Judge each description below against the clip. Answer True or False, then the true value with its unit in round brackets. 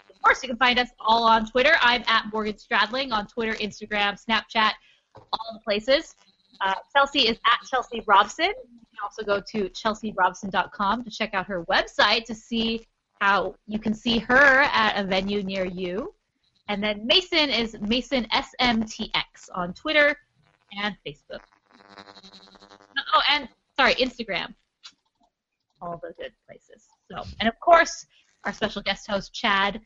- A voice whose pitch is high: True (220 Hz)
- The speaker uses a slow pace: False (155 wpm)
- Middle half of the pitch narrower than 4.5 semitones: True (4.0 semitones)